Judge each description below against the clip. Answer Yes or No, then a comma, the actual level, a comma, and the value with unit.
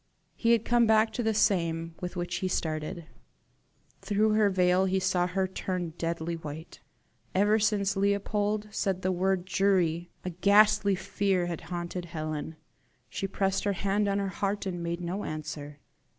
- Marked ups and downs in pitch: No, average, 2.8 semitones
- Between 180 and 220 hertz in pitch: Yes, high, 190 Hz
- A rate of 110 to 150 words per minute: No, average, 165 wpm